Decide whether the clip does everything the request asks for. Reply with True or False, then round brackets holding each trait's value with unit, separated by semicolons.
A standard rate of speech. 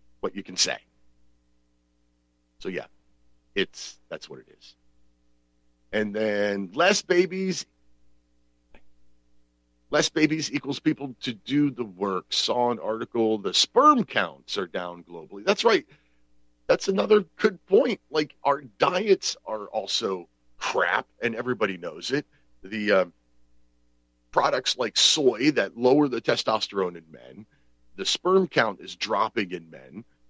False (130 wpm)